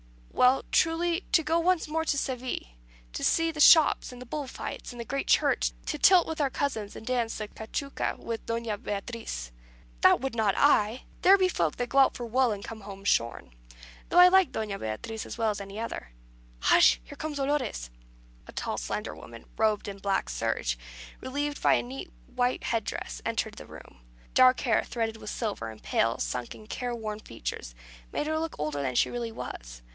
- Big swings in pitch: Yes, wide, 6.0 semitones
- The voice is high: Yes, high, 230 Hz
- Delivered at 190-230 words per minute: Yes, average, 200 wpm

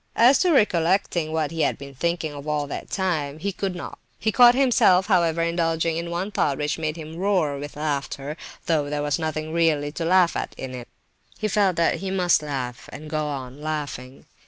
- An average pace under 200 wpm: No, fast, 205 wpm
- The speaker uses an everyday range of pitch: Yes, average, 3.5 semitones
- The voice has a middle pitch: Yes, medium, 160 Hz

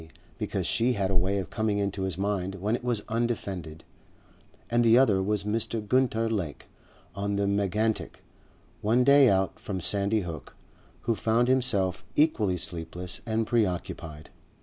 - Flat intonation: No, average, 3.3 semitones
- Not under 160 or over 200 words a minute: No, average, 150 wpm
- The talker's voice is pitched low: Yes, low, 100 Hz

